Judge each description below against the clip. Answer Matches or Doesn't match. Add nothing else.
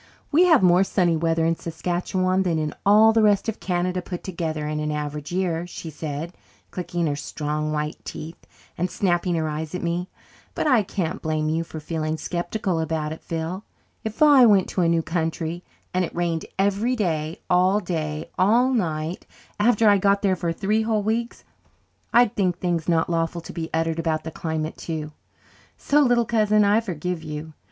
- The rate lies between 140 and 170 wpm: Doesn't match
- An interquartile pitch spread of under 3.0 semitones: Doesn't match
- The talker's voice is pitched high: Doesn't match